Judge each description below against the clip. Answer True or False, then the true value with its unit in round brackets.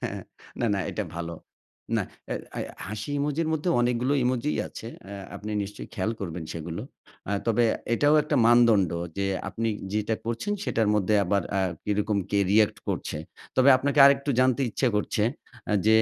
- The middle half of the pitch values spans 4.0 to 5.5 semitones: True (4.4 semitones)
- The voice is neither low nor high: False (110 Hz)